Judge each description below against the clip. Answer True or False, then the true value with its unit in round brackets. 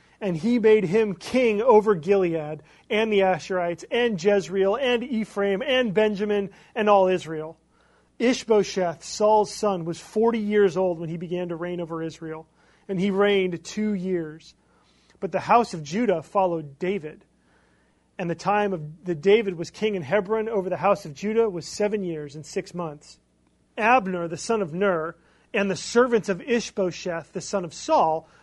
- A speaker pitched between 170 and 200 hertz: True (190 Hz)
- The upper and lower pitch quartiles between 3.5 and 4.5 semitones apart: True (4.0 semitones)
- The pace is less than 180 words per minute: True (165 wpm)